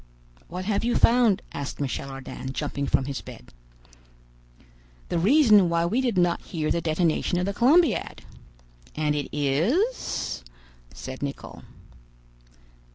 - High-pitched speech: No, medium, 170 Hz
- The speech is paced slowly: Yes, slow, 130 wpm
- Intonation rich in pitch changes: Yes, wide, 7.4 semitones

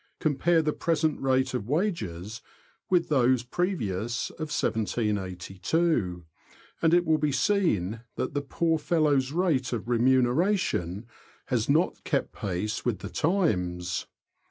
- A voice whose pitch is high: No, low, 130 Hz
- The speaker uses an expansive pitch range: Yes, wide, 7.5 semitones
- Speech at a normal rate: No, slow, 120 wpm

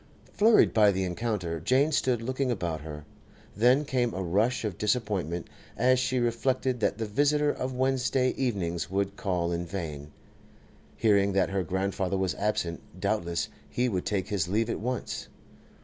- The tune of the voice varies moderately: No, wide, 5.8 semitones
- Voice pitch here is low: Yes, low, 105 Hz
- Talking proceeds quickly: No, average, 160 wpm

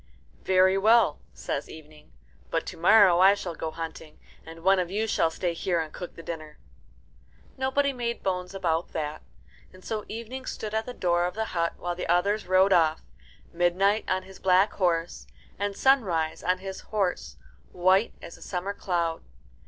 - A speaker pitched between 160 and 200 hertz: Yes, medium, 185 Hz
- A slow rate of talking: No, average, 175 wpm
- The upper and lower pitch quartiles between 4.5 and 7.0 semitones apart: No, average, 3.3 semitones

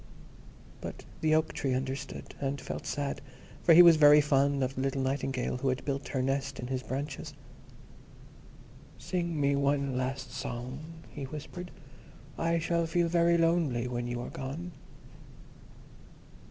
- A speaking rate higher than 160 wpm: No, average, 150 wpm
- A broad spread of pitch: No, average, 3.2 semitones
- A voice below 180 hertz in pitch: Yes, medium, 140 Hz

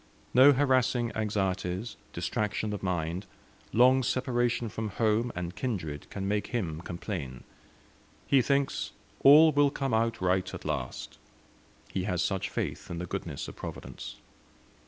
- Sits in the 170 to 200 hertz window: No, low, 105 Hz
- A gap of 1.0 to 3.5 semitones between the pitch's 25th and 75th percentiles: No, wide, 5.4 semitones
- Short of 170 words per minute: Yes, slow, 135 wpm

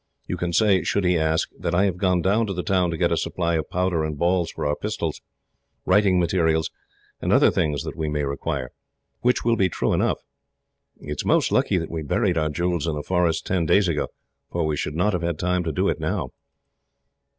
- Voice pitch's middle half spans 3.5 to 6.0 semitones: No, average, 2.7 semitones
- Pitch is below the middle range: Yes, very low, 85 Hz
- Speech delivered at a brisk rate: Yes, fast, 225 wpm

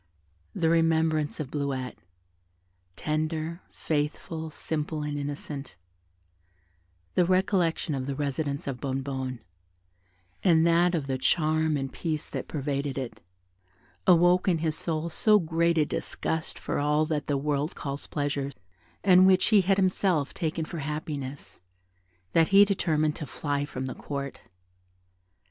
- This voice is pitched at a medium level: Yes, medium, 155 Hz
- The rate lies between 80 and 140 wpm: Yes, slow, 135 wpm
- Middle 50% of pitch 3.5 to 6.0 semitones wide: No, average, 2.8 semitones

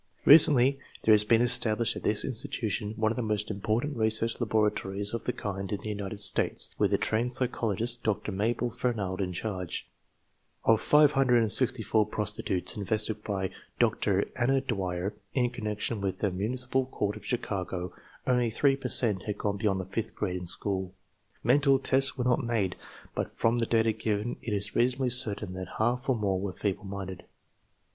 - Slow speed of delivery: No, average, 175 wpm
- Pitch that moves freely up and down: No, average, 3.4 semitones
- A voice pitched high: No, low, 110 Hz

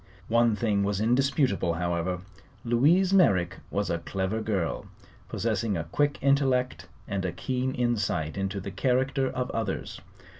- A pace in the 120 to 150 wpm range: Yes, average, 140 wpm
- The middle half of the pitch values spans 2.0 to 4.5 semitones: No, average, 5.3 semitones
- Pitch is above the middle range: No, low, 110 Hz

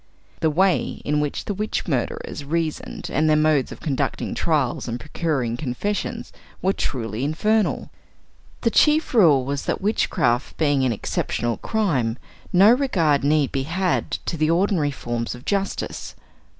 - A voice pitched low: No, medium, 155 Hz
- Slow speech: No, average, 150 wpm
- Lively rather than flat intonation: Yes, wide, 6.0 semitones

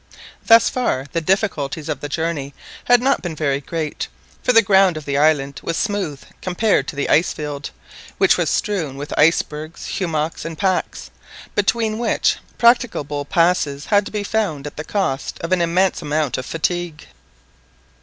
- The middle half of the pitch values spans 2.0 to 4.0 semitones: No, average, 5.0 semitones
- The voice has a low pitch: No, medium, 165 Hz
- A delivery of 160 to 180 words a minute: Yes, average, 165 wpm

